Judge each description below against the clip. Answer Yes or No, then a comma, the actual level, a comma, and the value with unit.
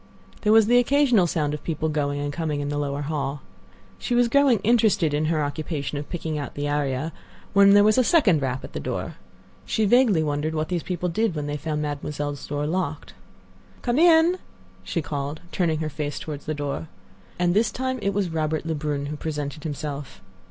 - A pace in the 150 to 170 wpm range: No, average, 200 wpm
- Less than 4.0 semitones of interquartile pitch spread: No, wide, 5.4 semitones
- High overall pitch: No, medium, 155 Hz